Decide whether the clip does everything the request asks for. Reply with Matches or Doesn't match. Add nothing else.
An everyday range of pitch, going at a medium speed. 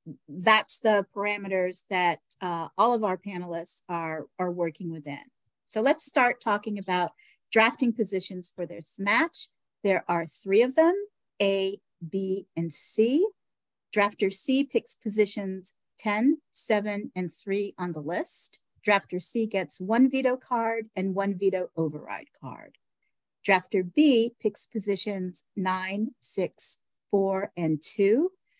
Doesn't match